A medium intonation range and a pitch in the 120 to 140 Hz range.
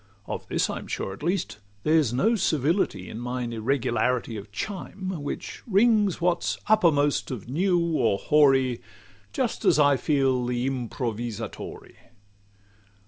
No: wide, 6.2 semitones; low, 135 Hz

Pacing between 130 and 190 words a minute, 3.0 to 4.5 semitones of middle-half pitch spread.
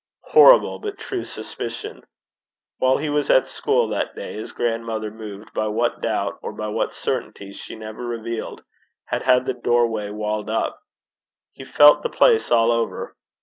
Yes: average, 160 wpm; average, 3.3 semitones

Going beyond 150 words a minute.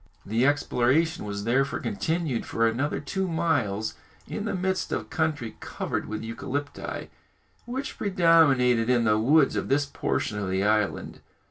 No: average, 145 wpm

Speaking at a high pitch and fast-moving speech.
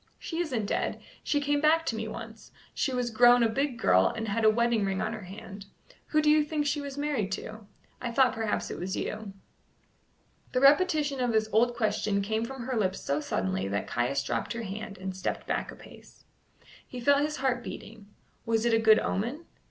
Yes: high, 225 Hz; fast, 210 wpm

